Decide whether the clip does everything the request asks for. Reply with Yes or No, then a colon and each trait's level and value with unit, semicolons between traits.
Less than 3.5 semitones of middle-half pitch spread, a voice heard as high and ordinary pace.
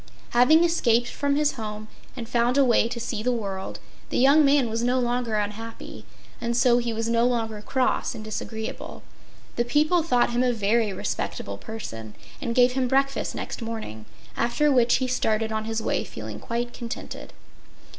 Yes: narrow, 2.4 semitones; high, 235 Hz; average, 175 wpm